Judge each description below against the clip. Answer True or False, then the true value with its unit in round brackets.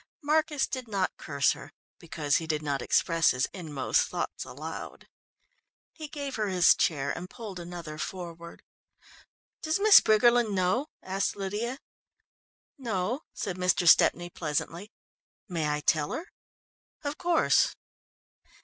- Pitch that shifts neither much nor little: False (6.7 semitones)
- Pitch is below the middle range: False (185 Hz)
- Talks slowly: True (130 wpm)